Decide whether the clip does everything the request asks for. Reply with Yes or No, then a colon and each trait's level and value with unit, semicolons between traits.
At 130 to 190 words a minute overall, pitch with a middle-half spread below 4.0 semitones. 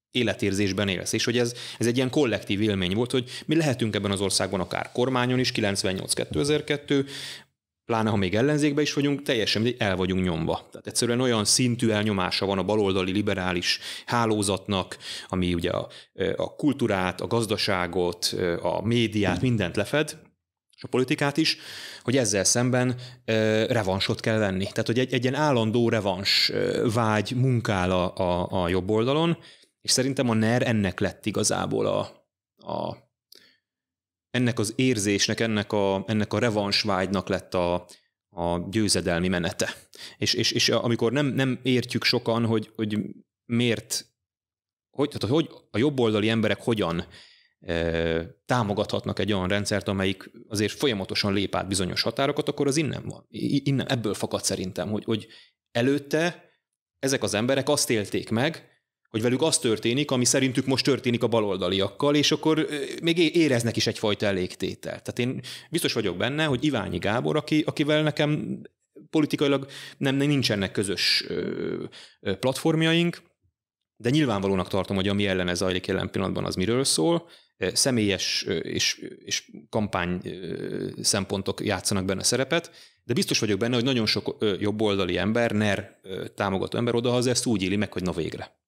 No: average, 145 wpm; average, 4.8 semitones